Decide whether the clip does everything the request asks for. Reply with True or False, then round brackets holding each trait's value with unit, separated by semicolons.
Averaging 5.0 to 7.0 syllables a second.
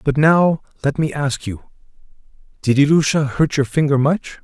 False (4.7 syllables/s)